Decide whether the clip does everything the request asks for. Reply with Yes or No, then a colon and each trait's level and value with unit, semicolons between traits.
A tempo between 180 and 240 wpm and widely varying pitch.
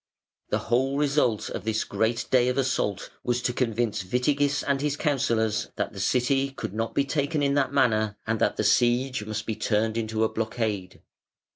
No: average, 185 wpm; average, 3.8 semitones